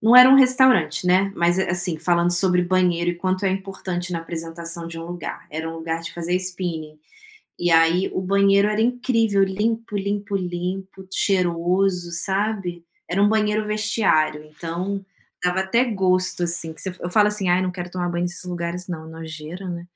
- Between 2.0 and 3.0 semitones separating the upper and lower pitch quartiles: Yes, narrow, 2.5 semitones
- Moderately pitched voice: Yes, medium, 180 Hz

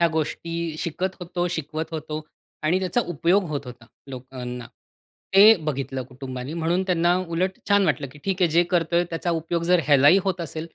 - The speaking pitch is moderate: Yes, medium, 165 Hz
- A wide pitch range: No, average, 3.3 semitones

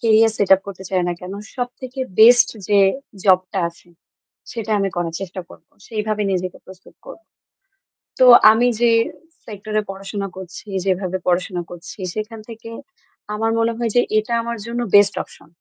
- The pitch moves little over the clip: No, average, 3.4 semitones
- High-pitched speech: Yes, high, 210 Hz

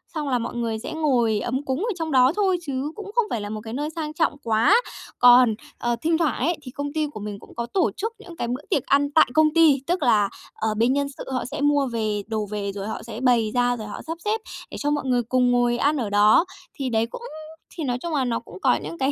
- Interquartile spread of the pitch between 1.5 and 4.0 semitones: No, average, 4.8 semitones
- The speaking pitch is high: Yes, very high, 260 Hz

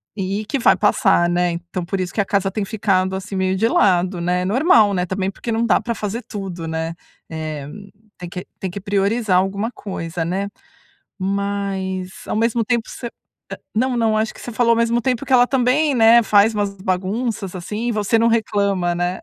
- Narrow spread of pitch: No, average, 3.7 semitones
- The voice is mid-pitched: No, high, 200 Hz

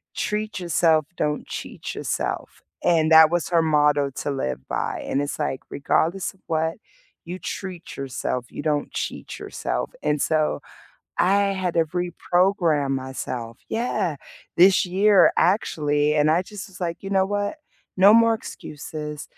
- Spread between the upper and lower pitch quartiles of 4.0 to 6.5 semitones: Yes, average, 4.3 semitones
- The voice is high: No, medium, 165 Hz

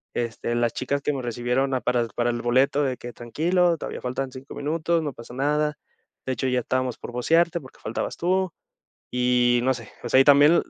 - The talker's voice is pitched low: Yes, low, 130 Hz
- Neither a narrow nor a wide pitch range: Yes, average, 3.3 semitones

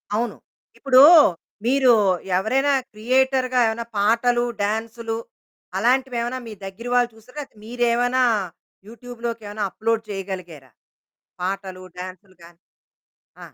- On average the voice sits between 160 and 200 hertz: No, high, 230 Hz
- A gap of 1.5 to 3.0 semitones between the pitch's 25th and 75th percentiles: No, average, 3.4 semitones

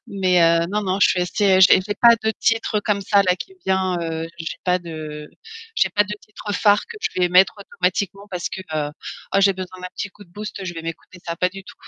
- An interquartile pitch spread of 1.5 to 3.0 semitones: Yes, narrow, 2.5 semitones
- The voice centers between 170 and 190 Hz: Yes, medium, 185 Hz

